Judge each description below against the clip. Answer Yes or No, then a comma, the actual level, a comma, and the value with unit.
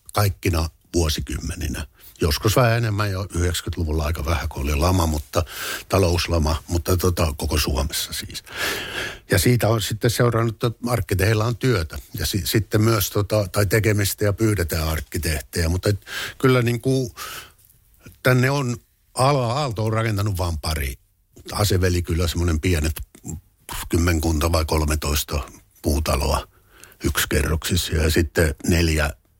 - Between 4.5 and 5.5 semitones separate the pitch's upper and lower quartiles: Yes, average, 4.9 semitones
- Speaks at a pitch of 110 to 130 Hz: No, very low, 90 Hz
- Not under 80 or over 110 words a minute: No, average, 120 wpm